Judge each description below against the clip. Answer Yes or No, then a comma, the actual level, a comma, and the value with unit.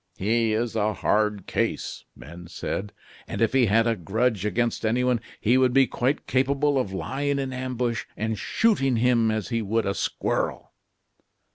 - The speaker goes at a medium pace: Yes, average, 165 wpm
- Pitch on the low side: Yes, low, 115 Hz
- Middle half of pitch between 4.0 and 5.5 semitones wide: No, average, 3.0 semitones